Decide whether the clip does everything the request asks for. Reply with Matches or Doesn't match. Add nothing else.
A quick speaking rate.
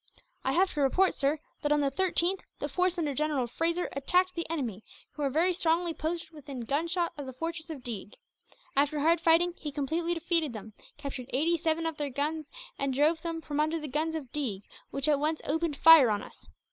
Matches